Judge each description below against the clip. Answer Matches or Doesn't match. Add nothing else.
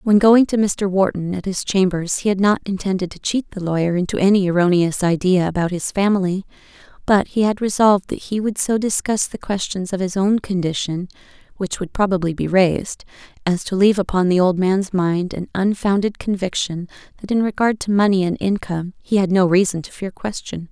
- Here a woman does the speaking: Matches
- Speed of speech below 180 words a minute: Doesn't match